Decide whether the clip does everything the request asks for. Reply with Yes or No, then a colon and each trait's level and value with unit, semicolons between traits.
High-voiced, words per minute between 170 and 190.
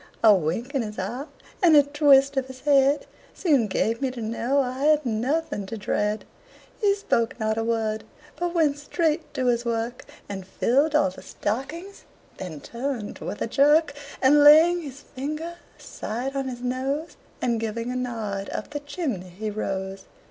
Yes: very high, 255 Hz; average, 175 wpm